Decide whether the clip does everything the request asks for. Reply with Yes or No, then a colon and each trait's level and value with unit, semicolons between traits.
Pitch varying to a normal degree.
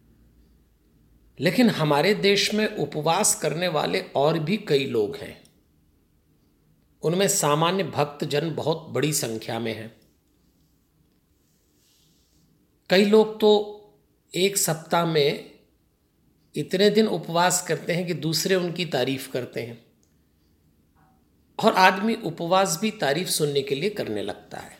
No: wide, 7.3 semitones